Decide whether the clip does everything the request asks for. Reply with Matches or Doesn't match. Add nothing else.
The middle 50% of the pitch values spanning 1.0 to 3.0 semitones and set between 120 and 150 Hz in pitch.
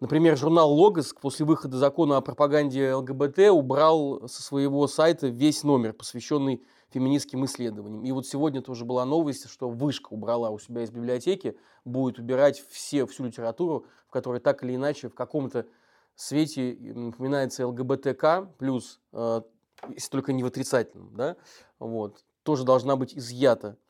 Matches